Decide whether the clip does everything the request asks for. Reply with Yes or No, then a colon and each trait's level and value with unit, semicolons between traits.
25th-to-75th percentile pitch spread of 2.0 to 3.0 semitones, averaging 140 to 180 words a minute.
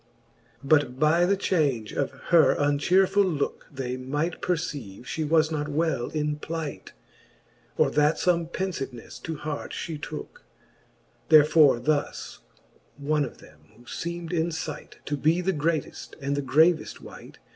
Yes: narrow, 2.6 semitones; average, 145 wpm